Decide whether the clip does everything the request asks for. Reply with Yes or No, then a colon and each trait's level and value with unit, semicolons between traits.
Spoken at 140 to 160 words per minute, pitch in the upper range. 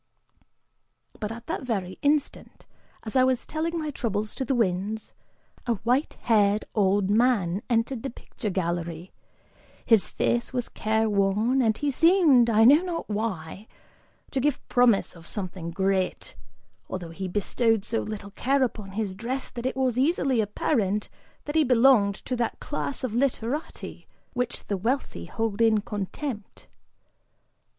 Yes: average, 150 wpm; high, 225 Hz